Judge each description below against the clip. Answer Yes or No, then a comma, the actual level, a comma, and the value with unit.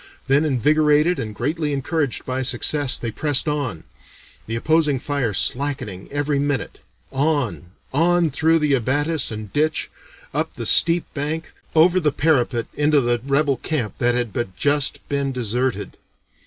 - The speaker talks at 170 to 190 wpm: No, average, 145 wpm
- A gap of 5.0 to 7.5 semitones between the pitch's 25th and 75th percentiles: No, average, 3.7 semitones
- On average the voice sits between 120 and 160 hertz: Yes, medium, 140 Hz